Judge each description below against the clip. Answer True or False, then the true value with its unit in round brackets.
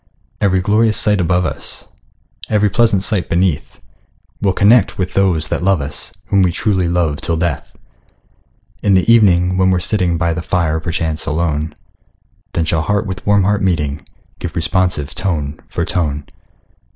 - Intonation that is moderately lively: True (3.3 semitones)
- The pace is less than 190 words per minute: True (160 wpm)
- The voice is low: True (90 Hz)